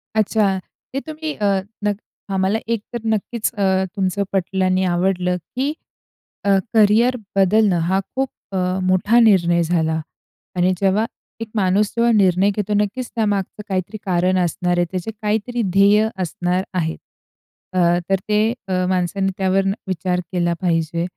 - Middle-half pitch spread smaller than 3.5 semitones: Yes, average, 2.8 semitones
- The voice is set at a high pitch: Yes, high, 195 Hz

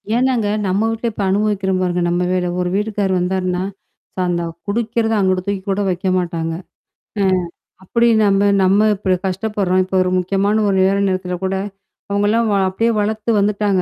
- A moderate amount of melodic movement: No, narrow, 2.3 semitones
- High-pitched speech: Yes, high, 195 Hz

